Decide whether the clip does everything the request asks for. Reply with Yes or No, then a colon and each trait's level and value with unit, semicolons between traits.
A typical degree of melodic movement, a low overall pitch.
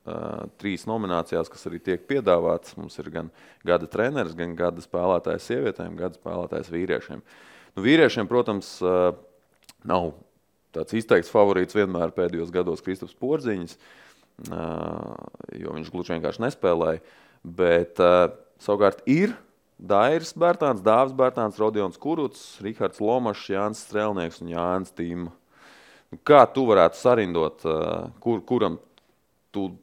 Yes: average, 3.8 semitones; very low, 90 Hz